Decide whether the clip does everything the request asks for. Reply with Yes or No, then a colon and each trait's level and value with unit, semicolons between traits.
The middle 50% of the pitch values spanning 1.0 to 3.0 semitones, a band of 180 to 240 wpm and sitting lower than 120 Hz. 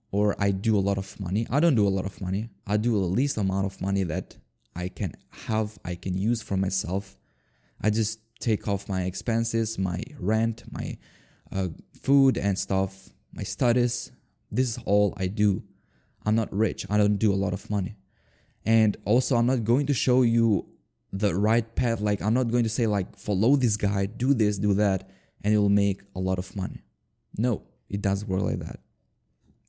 Yes: average, 2.7 semitones; average, 200 wpm; low, 105 Hz